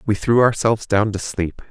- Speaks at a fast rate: Yes, fast, 210 wpm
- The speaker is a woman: No, male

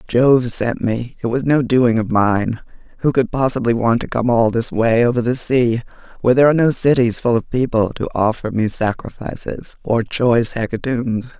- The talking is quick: No, average, 190 wpm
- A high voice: No, low, 120 Hz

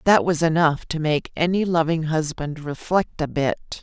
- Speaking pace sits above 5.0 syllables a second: No, 4.4 syllables/s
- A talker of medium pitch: Yes, medium, 160 Hz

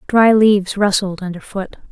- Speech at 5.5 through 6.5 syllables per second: No, 4.7 syllables/s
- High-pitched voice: Yes, high, 200 Hz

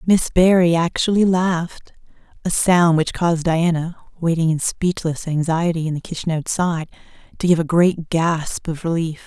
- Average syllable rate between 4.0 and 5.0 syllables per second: Yes, 4.9 syllables/s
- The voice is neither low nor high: Yes, medium, 170 Hz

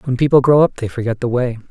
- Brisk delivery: Yes, fast, 280 wpm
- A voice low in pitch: Yes, low, 125 Hz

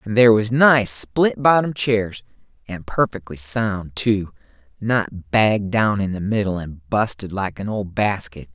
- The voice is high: No, low, 105 Hz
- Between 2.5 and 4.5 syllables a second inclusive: Yes, 4.1 syllables/s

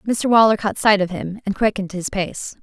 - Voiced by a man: No, female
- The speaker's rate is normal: No, fast, 230 wpm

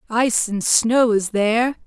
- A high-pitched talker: Yes, high, 225 Hz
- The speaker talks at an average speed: Yes, average, 160 wpm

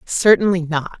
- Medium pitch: Yes, medium, 175 Hz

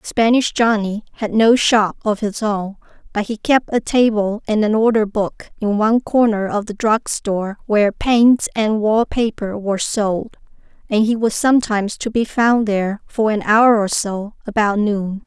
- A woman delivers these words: Yes, female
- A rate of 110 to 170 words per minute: No, average, 180 wpm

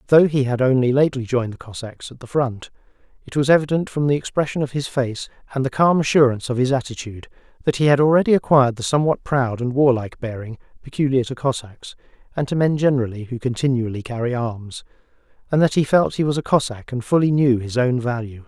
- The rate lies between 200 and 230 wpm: Yes, fast, 205 wpm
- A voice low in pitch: Yes, low, 130 Hz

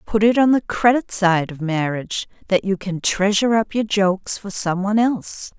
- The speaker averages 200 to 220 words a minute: Yes, fast, 205 wpm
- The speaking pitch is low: No, high, 200 Hz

